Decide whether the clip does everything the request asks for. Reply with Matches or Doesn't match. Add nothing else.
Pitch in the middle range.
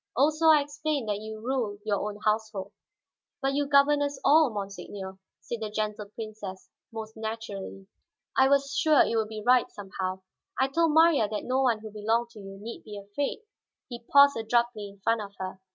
Doesn't match